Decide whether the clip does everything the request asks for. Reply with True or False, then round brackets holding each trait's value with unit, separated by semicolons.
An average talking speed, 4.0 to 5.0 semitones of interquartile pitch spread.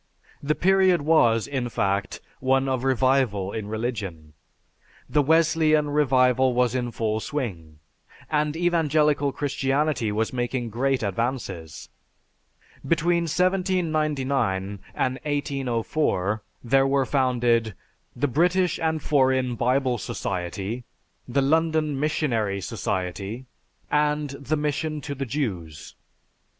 False (105 wpm; 4.7 semitones)